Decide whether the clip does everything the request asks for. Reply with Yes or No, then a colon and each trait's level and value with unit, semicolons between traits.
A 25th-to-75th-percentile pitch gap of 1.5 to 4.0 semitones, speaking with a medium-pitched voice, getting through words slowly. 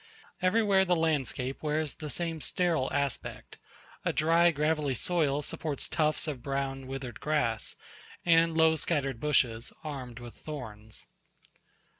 Yes: average, 3.3 semitones; medium, 150 Hz; slow, 125 wpm